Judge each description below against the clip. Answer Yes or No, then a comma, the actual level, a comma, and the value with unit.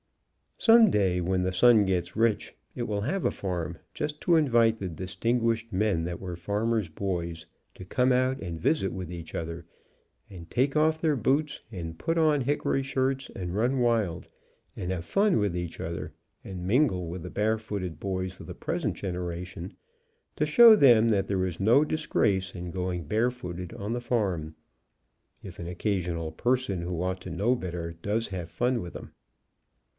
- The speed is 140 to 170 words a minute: No, average, 180 wpm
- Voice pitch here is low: Yes, low, 100 Hz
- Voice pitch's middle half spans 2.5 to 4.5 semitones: No, wide, 5.6 semitones